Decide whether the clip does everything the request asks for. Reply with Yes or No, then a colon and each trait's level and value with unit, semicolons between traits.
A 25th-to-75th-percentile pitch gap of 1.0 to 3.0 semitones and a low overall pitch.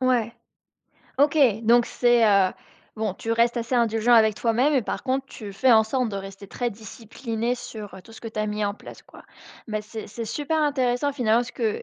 No: narrow, 2.5 semitones; high, 230 Hz